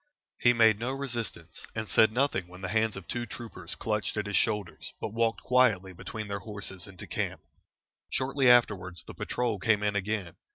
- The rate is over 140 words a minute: Yes, average, 180 wpm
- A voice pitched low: Yes, low, 110 Hz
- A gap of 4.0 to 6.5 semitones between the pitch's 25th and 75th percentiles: No, average, 3.4 semitones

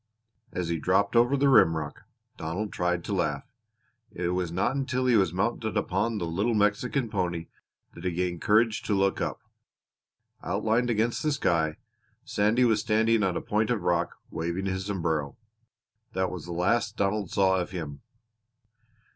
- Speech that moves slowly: No, average, 165 wpm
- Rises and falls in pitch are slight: No, average, 4.3 semitones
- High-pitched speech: No, very low, 95 Hz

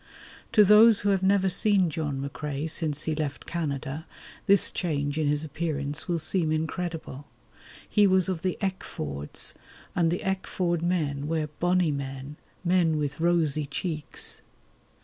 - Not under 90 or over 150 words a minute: Yes, average, 145 wpm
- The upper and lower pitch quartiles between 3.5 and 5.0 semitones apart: Yes, average, 3.8 semitones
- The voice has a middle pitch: Yes, medium, 160 Hz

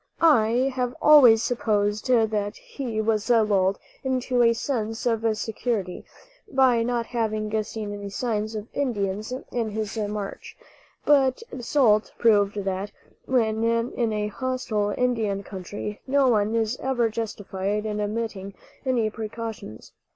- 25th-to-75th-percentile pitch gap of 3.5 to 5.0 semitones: No, average, 2.8 semitones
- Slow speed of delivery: Yes, slow, 130 wpm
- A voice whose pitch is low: No, high, 220 Hz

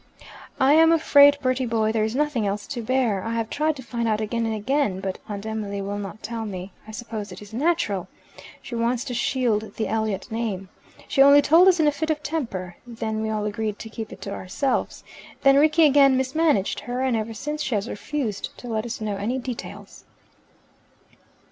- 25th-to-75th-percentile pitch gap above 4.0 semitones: Yes, average, 4.6 semitones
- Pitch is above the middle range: Yes, high, 230 Hz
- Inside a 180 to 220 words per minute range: Yes, fast, 205 wpm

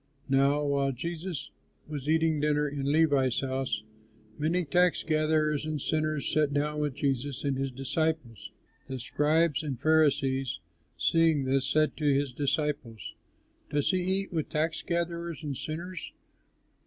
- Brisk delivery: No, average, 140 wpm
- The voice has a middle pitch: Yes, medium, 150 Hz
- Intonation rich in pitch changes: No, narrow, 2.5 semitones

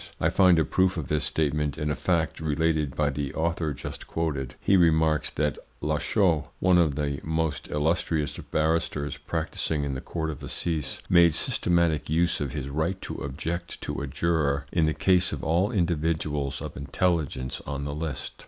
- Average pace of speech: Yes, average, 175 wpm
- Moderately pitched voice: No, very low, 80 Hz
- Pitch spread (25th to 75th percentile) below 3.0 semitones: Yes, narrow, 2.6 semitones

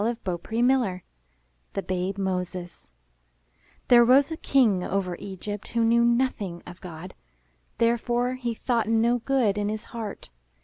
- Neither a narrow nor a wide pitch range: Yes, average, 4.2 semitones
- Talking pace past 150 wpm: No, average, 145 wpm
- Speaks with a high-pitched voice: Yes, high, 220 Hz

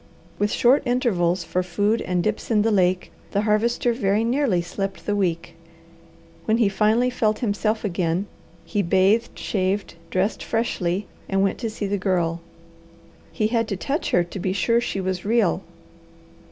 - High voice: Yes, high, 205 Hz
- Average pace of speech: Yes, average, 165 wpm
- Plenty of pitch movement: No, average, 3.4 semitones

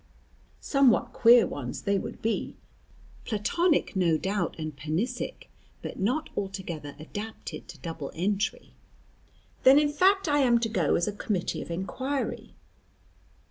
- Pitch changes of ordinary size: No, wide, 7.3 semitones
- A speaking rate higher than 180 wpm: No, slow, 135 wpm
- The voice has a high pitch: Yes, high, 205 Hz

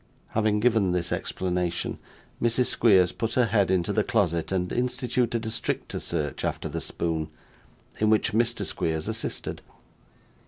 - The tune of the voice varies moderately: Yes, average, 4.7 semitones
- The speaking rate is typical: Yes, average, 145 wpm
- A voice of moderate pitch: No, low, 105 Hz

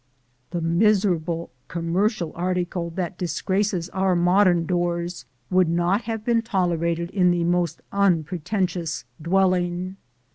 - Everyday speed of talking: No, slow, 110 wpm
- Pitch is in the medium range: Yes, medium, 180 Hz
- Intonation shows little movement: Yes, narrow, 2.1 semitones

